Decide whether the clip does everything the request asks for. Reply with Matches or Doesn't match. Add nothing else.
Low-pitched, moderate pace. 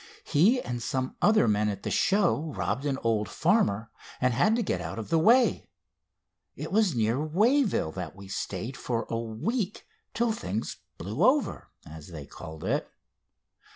Matches